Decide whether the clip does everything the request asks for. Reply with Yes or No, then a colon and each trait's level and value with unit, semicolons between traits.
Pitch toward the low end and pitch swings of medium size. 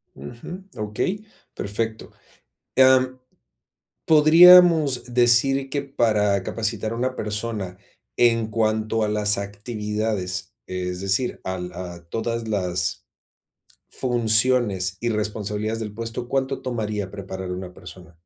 Yes: low, 110 Hz; average, 3.6 semitones